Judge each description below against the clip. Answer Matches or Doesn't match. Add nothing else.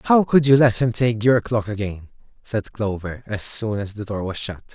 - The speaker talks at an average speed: Doesn't match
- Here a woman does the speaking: Doesn't match